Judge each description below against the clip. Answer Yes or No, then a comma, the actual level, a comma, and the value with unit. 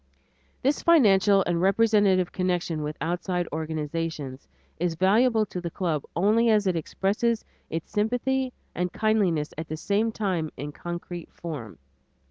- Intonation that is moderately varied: Yes, average, 4.6 semitones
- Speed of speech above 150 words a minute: No, slow, 135 wpm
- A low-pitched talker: No, medium, 180 Hz